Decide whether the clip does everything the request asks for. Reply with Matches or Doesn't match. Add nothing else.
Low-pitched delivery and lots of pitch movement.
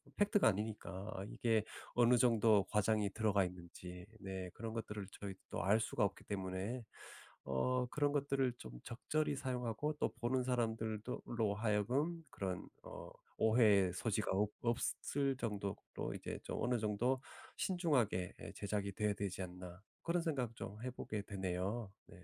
Doesn't match